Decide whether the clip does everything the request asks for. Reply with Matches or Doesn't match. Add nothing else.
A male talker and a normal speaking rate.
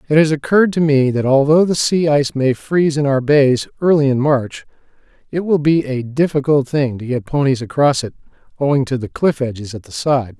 Doesn't match